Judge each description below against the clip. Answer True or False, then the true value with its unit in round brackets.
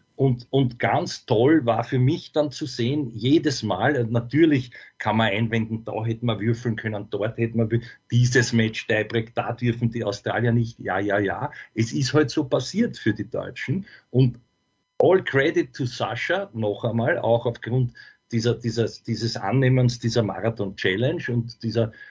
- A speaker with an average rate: True (170 wpm)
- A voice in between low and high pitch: False (120 Hz)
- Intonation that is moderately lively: False (2.3 semitones)